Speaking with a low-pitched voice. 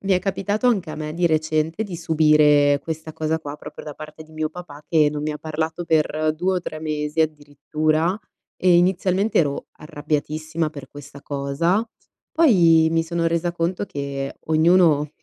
No: medium, 155 Hz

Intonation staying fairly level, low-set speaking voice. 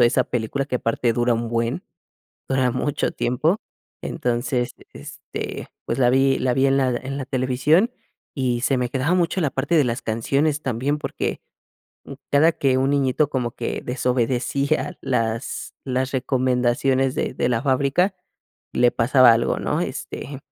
Yes: narrow, 2.2 semitones; low, 130 Hz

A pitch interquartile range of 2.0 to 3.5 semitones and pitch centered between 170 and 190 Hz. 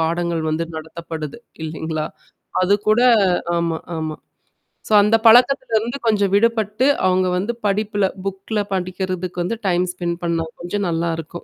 No: average, 3.9 semitones; medium, 185 Hz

